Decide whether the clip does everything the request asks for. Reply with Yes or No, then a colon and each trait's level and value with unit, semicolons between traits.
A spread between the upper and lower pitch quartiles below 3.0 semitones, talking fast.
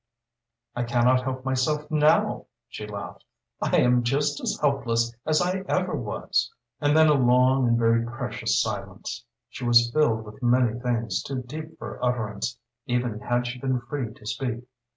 No: narrow, 2.5 semitones; average, 170 wpm